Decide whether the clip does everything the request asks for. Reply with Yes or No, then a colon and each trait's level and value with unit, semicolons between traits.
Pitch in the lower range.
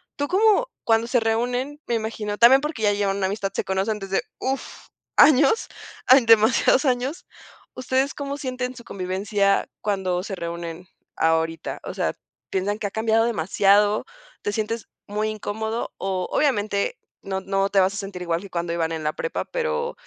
No: high, 210 Hz